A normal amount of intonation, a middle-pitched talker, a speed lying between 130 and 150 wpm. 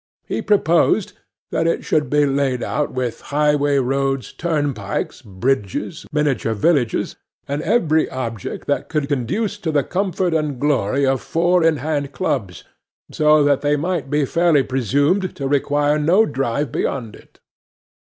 Yes: average, 3.0 semitones; medium, 145 Hz; average, 145 wpm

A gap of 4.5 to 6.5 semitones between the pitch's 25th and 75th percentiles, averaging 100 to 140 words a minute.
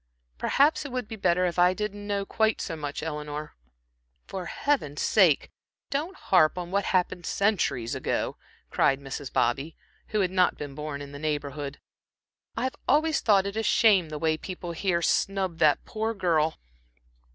No: average, 5.3 semitones; average, 165 wpm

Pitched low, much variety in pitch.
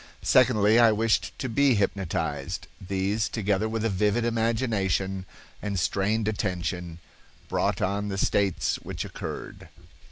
No: low, 105 Hz; average, 2.8 semitones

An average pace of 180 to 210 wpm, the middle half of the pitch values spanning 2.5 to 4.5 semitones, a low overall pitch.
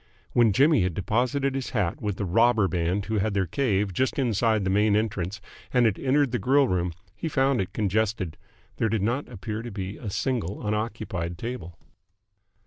Yes: average, 185 wpm; average, 4.2 semitones; low, 110 Hz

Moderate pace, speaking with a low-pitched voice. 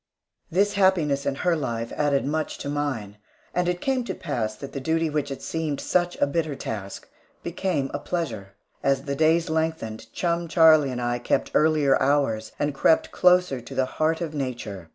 No: average, 185 wpm; medium, 145 Hz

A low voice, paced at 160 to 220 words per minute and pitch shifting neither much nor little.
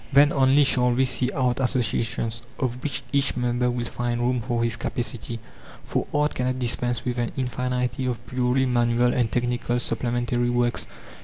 No: low, 125 Hz; average, 165 wpm; narrow, 1.1 semitones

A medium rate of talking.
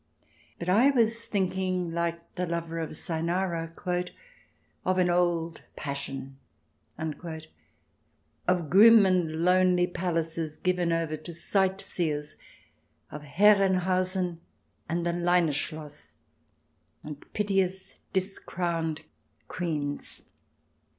No: slow, 90 wpm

